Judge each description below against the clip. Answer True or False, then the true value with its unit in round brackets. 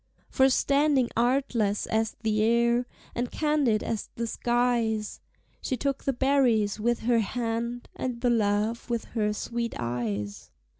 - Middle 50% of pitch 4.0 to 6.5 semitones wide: False (2.4 semitones)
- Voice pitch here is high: True (235 Hz)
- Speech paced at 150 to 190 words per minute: False (140 wpm)